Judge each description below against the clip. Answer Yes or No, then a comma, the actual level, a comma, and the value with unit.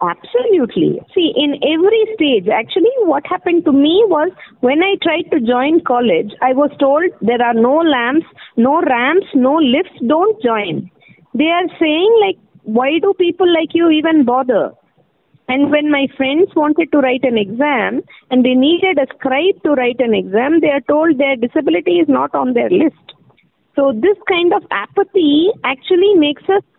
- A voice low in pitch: No, very high, 305 Hz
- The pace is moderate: Yes, average, 170 wpm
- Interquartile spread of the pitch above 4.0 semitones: Yes, average, 5.1 semitones